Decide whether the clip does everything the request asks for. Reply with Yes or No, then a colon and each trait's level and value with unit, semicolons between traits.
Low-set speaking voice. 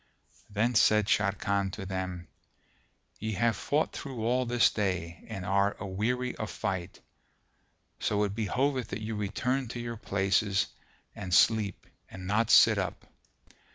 Yes: low, 105 Hz